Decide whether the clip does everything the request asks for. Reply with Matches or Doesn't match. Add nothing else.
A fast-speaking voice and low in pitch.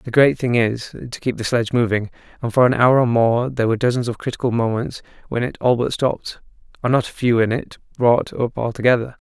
Matches